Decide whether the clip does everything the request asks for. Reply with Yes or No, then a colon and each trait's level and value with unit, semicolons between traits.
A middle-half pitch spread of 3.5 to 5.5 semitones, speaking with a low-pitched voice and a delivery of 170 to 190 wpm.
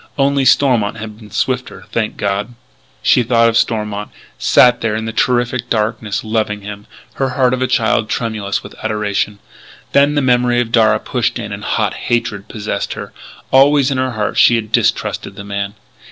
No: average, 3.1 semitones; low, 115 Hz; average, 180 wpm